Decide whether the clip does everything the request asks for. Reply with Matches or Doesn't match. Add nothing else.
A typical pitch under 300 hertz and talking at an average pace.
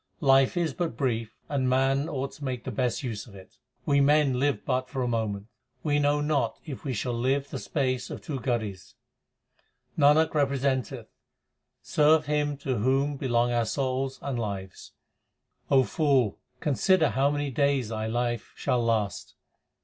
Matches